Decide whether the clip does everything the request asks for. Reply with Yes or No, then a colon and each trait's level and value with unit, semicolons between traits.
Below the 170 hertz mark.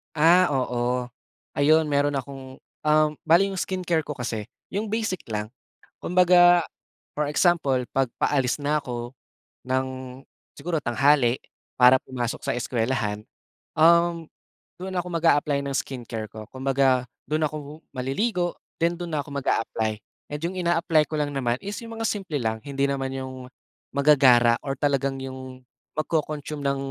Yes: medium, 140 Hz